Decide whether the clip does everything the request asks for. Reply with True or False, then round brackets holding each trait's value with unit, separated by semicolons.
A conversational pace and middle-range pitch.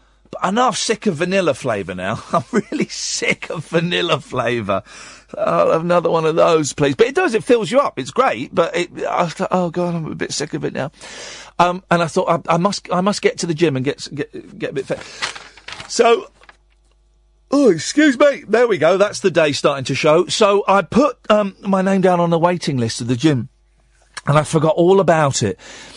False (220 wpm; 175 Hz)